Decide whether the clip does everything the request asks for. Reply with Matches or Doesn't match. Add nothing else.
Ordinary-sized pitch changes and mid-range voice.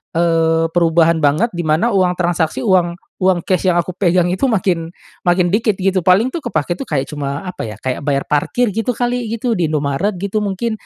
Matches